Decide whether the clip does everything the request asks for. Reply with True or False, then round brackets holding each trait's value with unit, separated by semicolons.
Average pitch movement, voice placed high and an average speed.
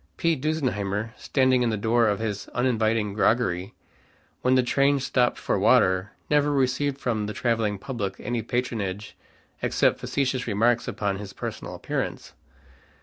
False (3.8 semitones; 115 Hz; 145 wpm)